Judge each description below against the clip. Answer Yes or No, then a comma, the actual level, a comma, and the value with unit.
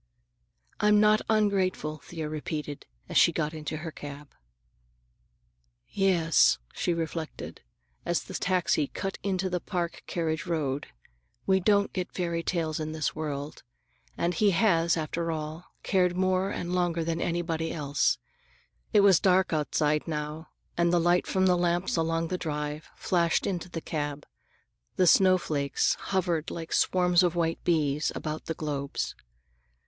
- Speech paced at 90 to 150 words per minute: Yes, average, 145 wpm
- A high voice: No, medium, 170 Hz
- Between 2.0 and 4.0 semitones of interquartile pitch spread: Yes, average, 2.8 semitones